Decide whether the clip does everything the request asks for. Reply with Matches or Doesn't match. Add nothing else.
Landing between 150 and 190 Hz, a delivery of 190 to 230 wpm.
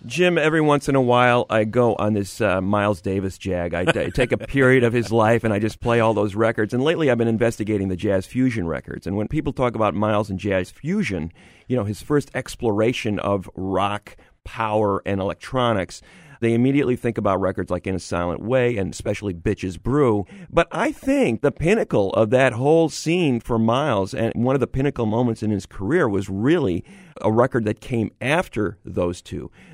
Doesn't match